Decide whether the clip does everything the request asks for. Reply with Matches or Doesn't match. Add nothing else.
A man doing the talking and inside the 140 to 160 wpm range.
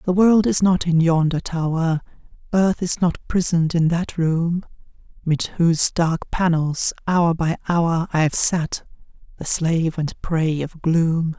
Doesn't match